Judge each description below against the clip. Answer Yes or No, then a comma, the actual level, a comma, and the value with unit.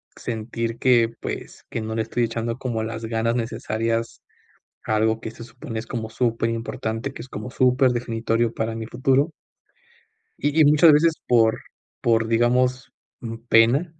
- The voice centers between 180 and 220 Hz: No, low, 115 Hz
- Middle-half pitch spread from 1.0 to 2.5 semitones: Yes, narrow, 2.0 semitones